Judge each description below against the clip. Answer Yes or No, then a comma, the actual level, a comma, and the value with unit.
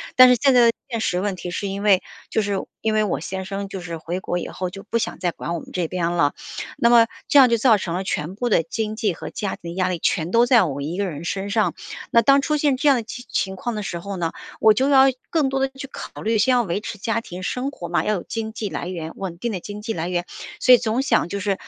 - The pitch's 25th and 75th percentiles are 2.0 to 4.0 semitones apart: No, average, 4.8 semitones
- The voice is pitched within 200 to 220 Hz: Yes, high, 205 Hz